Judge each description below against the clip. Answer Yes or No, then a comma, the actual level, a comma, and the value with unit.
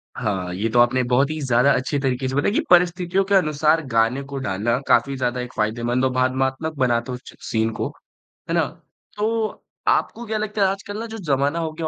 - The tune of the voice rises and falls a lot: Yes, wide, 6.0 semitones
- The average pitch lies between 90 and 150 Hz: Yes, low, 135 Hz